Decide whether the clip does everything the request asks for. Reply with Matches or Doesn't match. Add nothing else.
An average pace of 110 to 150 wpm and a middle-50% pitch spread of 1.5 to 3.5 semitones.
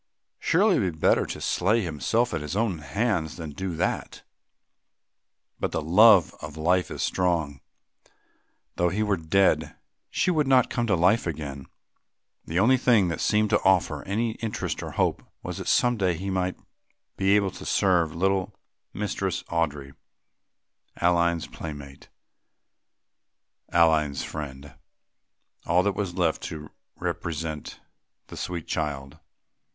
Doesn't match